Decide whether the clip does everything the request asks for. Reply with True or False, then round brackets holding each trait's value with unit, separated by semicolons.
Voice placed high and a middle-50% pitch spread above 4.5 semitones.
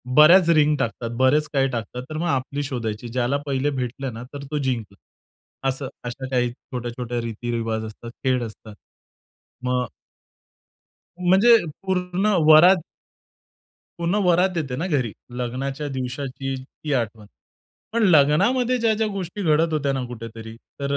False (135 Hz; 5.2 semitones)